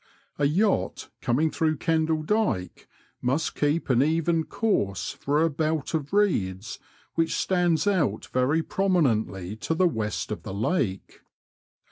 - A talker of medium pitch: Yes, medium, 155 Hz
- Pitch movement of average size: No, wide, 5.7 semitones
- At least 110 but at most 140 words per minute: Yes, slow, 135 wpm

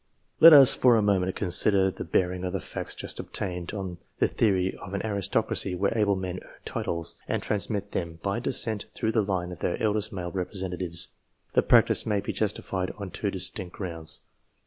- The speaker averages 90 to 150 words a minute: No, average, 190 wpm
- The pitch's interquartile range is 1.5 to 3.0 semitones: Yes, narrow, 2.4 semitones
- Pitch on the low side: Yes, very low, 95 Hz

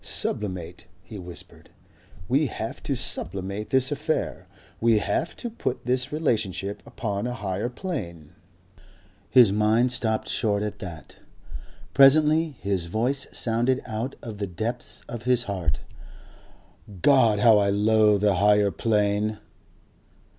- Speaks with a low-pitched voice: Yes, low, 110 Hz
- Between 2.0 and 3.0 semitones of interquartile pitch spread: No, average, 3.8 semitones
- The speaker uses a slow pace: Yes, slow, 125 wpm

